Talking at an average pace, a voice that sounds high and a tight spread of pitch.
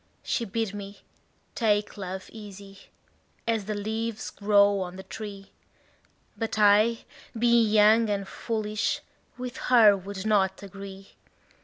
No: slow, 125 wpm; high, 205 Hz; narrow, 2.0 semitones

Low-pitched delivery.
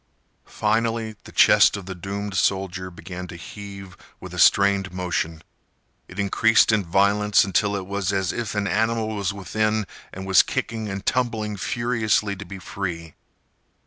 Yes: low, 100 Hz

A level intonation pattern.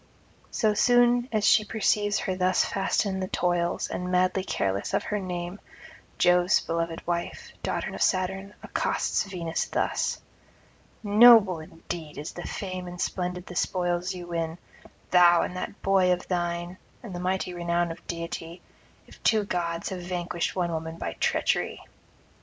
Yes: narrow, 2.0 semitones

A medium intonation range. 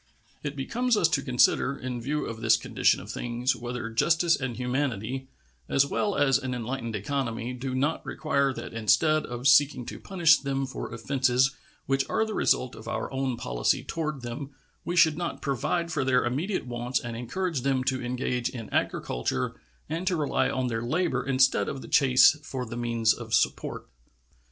Yes: average, 3.3 semitones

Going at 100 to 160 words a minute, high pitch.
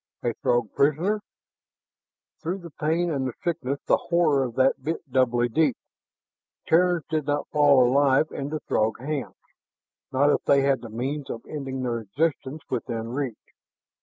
No: average, 155 wpm; medium, 140 Hz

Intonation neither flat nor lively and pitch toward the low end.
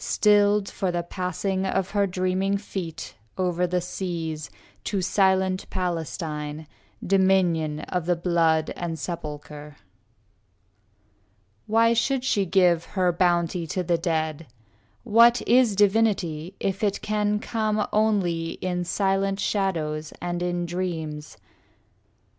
No: average, 3.1 semitones; medium, 180 Hz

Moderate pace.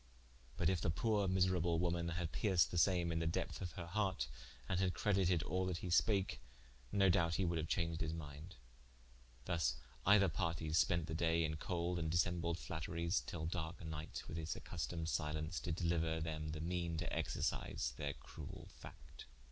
Yes: average, 180 wpm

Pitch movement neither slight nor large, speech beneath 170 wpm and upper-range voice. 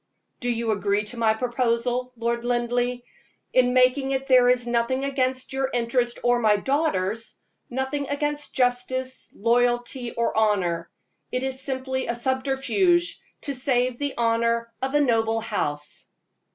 No: narrow, 2.1 semitones; average, 140 wpm; high, 245 Hz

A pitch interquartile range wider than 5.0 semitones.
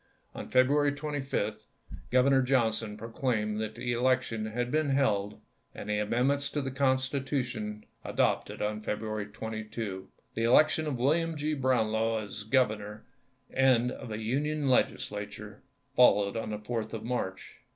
No: average, 3.7 semitones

